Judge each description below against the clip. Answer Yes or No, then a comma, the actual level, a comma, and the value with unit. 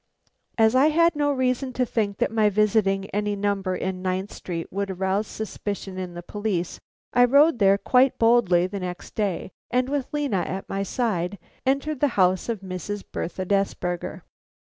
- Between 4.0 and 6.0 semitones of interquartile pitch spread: Yes, average, 4.6 semitones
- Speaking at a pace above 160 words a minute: Yes, average, 170 wpm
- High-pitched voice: Yes, high, 205 Hz